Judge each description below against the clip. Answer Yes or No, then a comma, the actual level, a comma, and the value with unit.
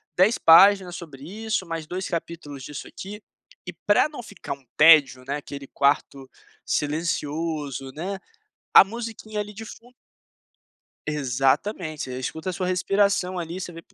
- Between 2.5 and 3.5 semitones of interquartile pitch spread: No, average, 5.2 semitones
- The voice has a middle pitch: Yes, medium, 165 Hz